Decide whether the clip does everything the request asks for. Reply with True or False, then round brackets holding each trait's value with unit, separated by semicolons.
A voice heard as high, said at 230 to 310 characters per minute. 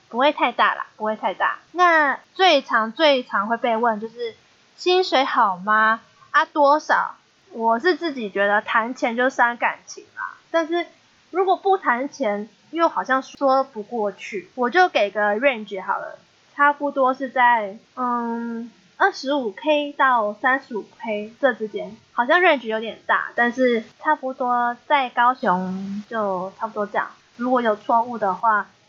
True (245 Hz; 235 characters per minute)